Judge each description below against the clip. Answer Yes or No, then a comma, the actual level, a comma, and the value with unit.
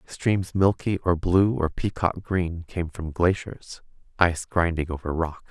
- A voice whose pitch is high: No, very low, 85 Hz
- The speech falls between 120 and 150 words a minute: Yes, average, 140 wpm